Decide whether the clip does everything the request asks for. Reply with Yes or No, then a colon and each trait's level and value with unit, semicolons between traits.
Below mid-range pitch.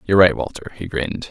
Yes: very low, 90 Hz